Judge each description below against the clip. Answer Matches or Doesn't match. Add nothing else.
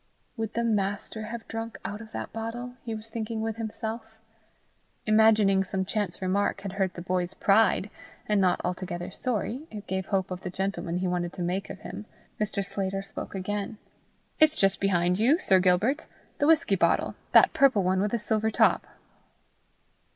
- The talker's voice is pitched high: Matches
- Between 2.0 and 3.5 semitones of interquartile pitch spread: Matches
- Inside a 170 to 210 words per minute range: Matches